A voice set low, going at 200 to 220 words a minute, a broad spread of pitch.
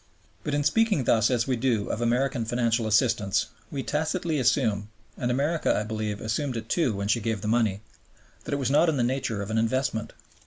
No: low, 120 Hz; fast, 205 wpm; average, 3.8 semitones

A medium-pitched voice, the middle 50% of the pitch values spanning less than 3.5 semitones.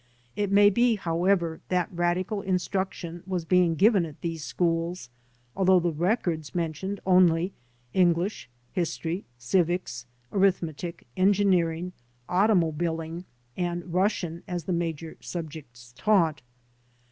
Yes: medium, 175 Hz; narrow, 2.4 semitones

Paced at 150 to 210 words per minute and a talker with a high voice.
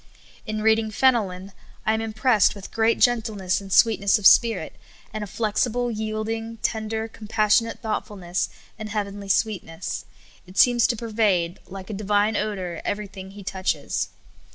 Yes: average, 155 wpm; high, 215 Hz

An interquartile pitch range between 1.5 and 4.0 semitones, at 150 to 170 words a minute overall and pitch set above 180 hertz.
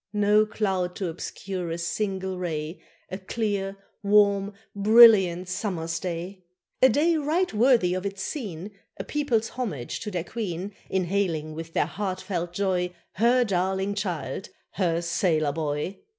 No: average, 3.5 semitones; average, 140 wpm; high, 190 Hz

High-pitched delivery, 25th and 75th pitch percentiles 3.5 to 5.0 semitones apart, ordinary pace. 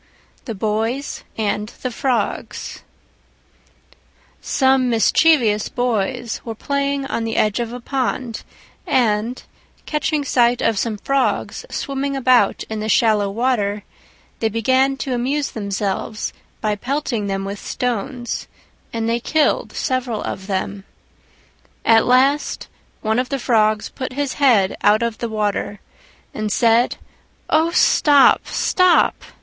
No: high, 235 Hz; average, 3.8 semitones; slow, 125 wpm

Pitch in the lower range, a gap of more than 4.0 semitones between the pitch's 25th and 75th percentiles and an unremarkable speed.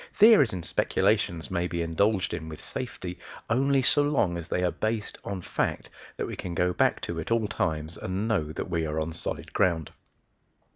Yes: very low, 90 Hz; average, 5.1 semitones; average, 195 wpm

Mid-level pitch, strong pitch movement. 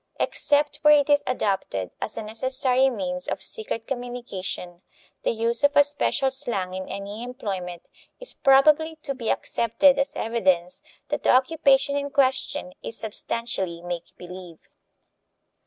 No: high, 240 Hz; wide, 6.7 semitones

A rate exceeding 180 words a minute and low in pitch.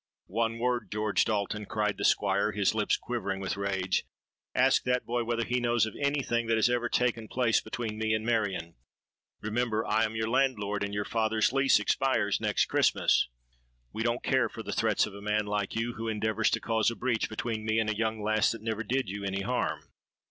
Yes: fast, 205 wpm; low, 110 Hz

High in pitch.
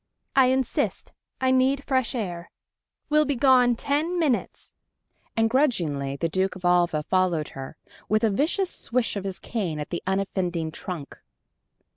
Yes: high, 205 Hz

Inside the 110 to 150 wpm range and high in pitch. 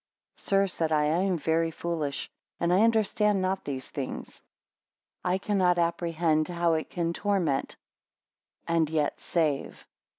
No: slow, 135 wpm; medium, 170 Hz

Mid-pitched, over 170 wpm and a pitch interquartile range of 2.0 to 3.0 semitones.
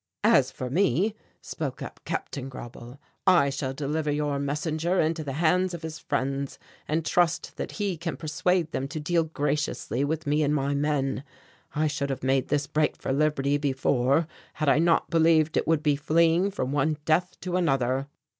Yes: medium, 150 Hz; average, 180 wpm; average, 2.7 semitones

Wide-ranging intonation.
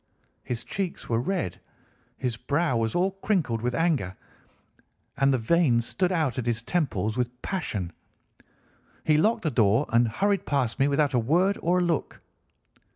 Yes: wide, 6.8 semitones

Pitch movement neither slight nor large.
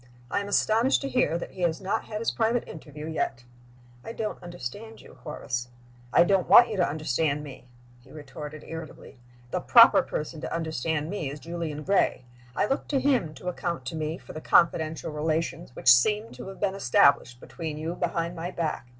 Yes: average, 4.3 semitones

